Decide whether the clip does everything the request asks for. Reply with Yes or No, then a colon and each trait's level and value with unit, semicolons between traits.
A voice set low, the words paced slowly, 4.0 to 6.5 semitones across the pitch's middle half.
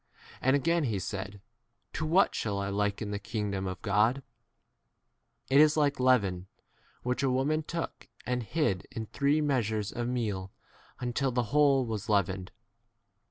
No: low, 120 Hz; average, 155 wpm; wide, 5.4 semitones